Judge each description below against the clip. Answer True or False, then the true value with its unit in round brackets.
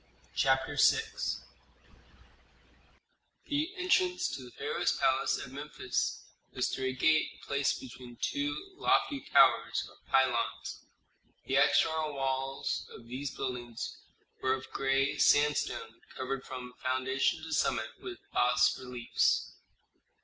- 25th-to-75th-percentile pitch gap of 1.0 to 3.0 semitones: True (2.7 semitones)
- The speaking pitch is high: False (135 Hz)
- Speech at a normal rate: False (115 wpm)